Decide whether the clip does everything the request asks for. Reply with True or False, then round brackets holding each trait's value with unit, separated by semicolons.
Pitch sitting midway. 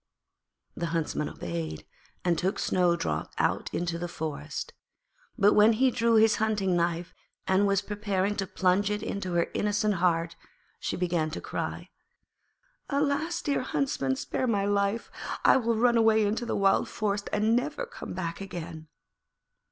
False (200 Hz)